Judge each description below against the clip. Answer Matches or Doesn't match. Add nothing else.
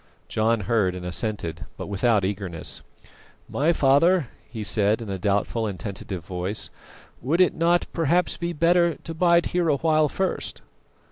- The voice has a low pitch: Matches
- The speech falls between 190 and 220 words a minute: Doesn't match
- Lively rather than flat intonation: Matches